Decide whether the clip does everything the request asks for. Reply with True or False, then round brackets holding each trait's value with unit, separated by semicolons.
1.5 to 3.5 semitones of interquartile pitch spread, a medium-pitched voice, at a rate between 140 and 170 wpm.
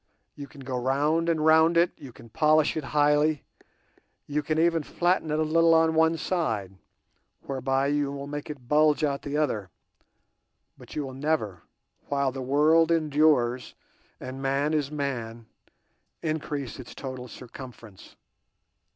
True (2.9 semitones; 145 Hz; 150 wpm)